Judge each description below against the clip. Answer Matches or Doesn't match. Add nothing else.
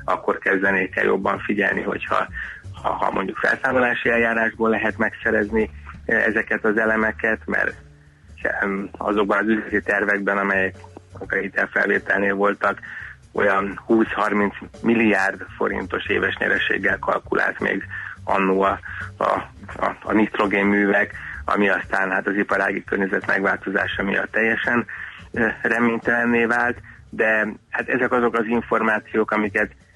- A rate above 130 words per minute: Doesn't match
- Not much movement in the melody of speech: Matches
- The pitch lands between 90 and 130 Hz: Matches